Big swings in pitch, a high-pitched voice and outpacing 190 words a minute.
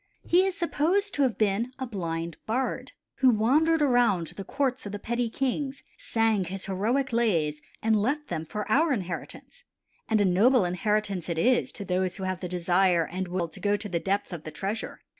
Yes: wide, 5.8 semitones; high, 210 Hz; average, 200 wpm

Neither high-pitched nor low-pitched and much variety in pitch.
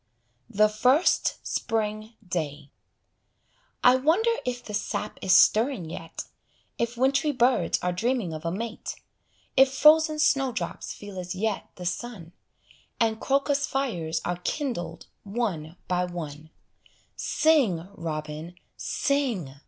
No: high, 215 Hz; wide, 7.0 semitones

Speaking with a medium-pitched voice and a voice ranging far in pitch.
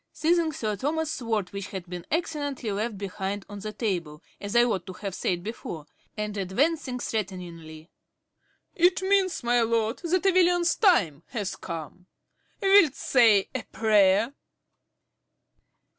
No: high, 215 Hz; wide, 7.7 semitones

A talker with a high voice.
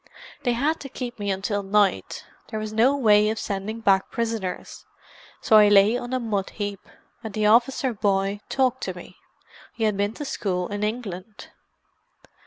Yes: high, 215 Hz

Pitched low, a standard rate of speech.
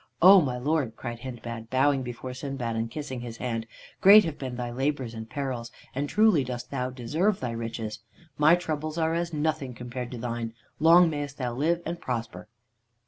Yes: low, 130 Hz; average, 185 wpm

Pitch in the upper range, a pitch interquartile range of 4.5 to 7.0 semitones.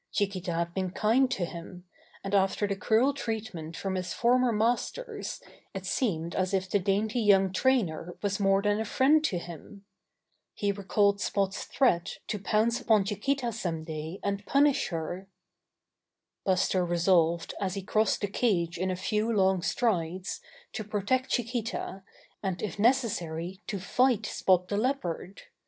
No: high, 200 Hz; average, 3.6 semitones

